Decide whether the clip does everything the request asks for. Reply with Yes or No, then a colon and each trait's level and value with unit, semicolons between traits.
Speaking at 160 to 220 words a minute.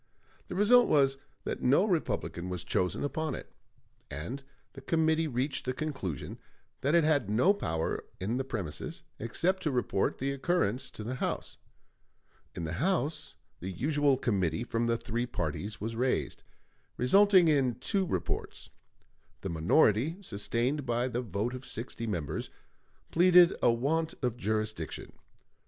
No: average, 145 wpm